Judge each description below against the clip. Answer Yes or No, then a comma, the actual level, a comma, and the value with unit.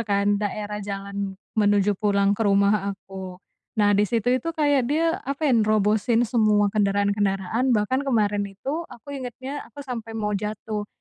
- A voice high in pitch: Yes, high, 210 Hz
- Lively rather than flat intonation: No, average, 3.3 semitones